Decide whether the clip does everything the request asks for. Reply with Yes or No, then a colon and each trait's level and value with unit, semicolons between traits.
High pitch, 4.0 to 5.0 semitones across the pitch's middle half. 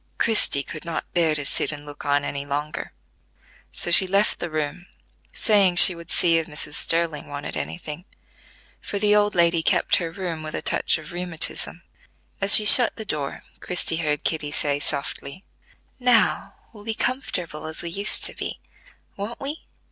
No: medium, 170 Hz; average, 4.6 semitones